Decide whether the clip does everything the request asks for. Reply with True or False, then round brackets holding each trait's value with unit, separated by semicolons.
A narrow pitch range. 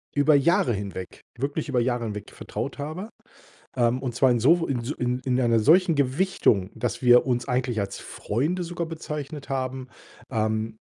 False (4.2 semitones)